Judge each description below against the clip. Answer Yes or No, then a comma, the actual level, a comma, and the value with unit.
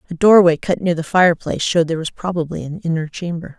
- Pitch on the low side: No, medium, 170 Hz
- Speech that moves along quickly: Yes, fast, 220 wpm